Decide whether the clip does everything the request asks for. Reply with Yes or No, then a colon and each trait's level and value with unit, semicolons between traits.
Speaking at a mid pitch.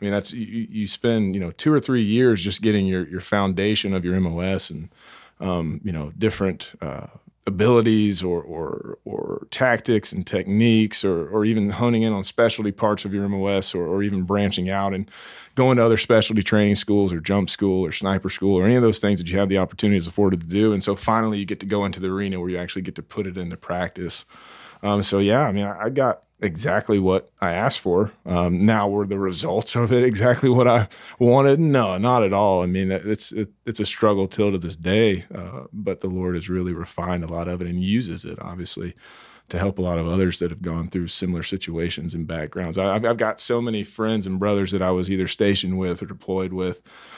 No: low, 100 Hz